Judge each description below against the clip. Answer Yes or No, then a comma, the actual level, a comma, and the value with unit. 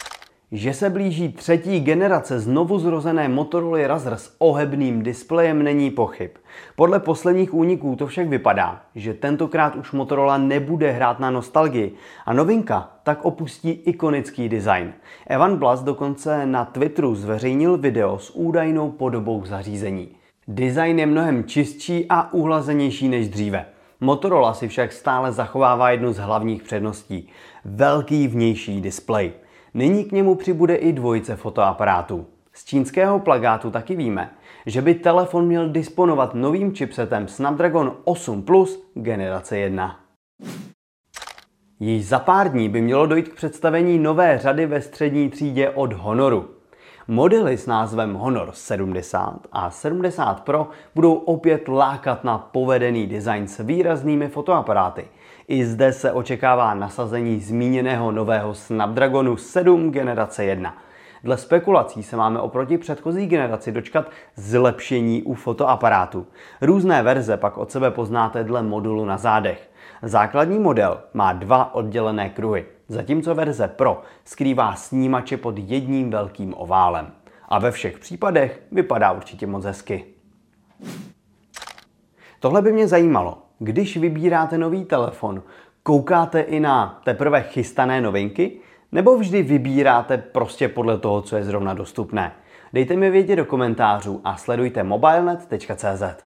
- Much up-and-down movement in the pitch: Yes, wide, 6.2 semitones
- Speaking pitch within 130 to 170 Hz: Yes, low, 135 Hz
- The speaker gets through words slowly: No, average, 130 wpm